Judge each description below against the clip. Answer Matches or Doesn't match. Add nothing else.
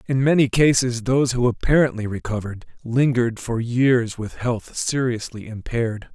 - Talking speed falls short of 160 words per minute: Matches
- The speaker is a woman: Doesn't match